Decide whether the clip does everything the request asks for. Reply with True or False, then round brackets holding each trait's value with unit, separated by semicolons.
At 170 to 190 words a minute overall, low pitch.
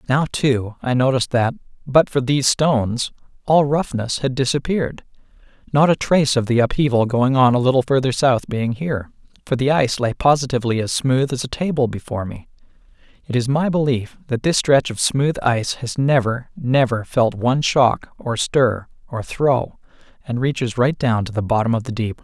True (185 wpm; 130 Hz)